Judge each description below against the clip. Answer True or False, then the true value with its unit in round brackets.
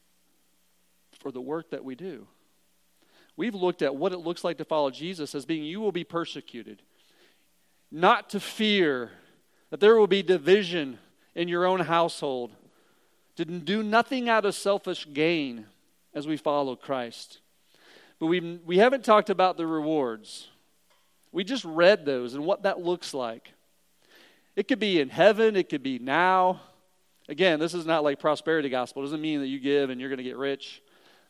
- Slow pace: False (175 wpm)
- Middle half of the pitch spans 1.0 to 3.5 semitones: False (5.1 semitones)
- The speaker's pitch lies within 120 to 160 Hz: False (170 Hz)